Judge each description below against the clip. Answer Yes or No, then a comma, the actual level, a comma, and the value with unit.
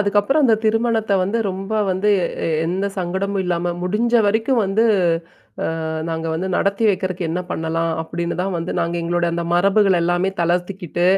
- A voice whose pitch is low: No, medium, 185 Hz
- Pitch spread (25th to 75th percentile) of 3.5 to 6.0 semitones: No, average, 2.9 semitones